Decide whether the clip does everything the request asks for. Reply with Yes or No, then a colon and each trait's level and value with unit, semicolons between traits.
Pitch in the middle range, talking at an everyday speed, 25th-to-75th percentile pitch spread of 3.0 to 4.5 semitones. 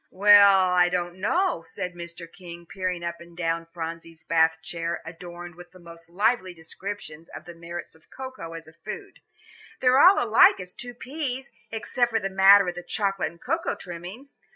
Yes: medium, 175 Hz; average, 180 wpm; average, 3.4 semitones